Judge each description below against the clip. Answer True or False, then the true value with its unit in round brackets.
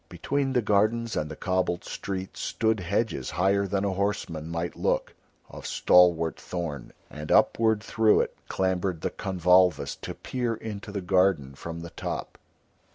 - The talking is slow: False (155 wpm)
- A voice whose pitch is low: True (95 Hz)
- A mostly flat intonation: False (3.6 semitones)